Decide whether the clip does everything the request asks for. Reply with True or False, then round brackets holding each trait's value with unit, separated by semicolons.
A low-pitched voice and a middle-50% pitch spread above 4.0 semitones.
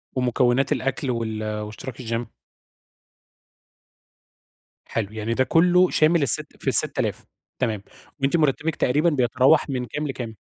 True (130 Hz; 4.4 semitones)